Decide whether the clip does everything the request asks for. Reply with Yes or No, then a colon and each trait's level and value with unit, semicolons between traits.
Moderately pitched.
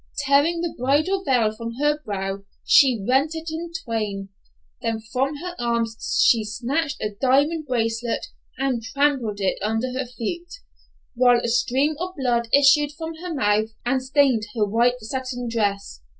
No: very high, 250 Hz